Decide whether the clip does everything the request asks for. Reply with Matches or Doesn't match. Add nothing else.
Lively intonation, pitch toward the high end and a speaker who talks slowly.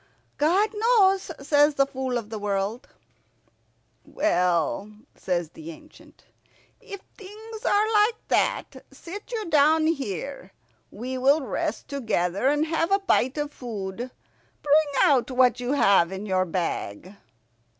Matches